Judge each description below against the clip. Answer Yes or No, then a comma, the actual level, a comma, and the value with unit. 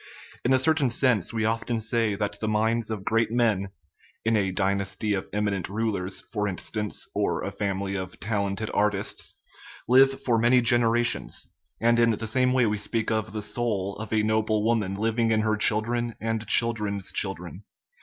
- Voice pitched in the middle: No, low, 110 Hz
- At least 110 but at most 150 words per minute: No, average, 180 wpm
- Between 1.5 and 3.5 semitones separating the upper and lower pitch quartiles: Yes, narrow, 2.5 semitones